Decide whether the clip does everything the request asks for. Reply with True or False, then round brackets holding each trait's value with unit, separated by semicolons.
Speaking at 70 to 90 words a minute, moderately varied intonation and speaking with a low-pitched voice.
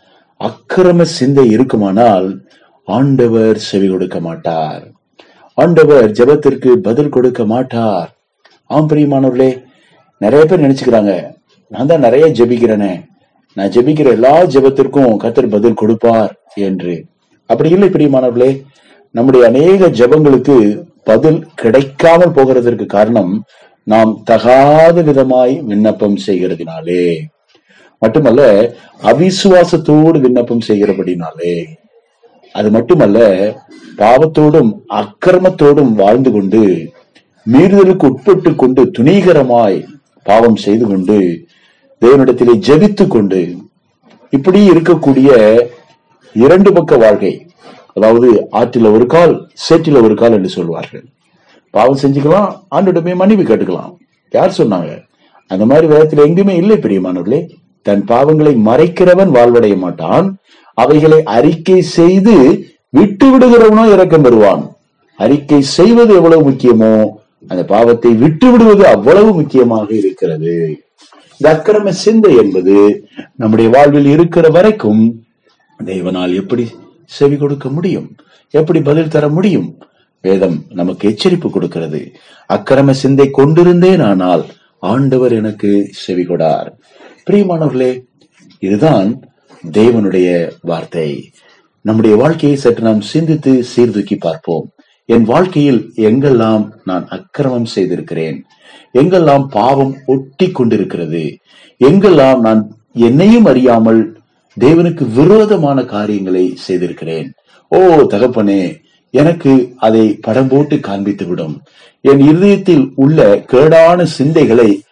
False (85 wpm; 6.9 semitones; 130 Hz)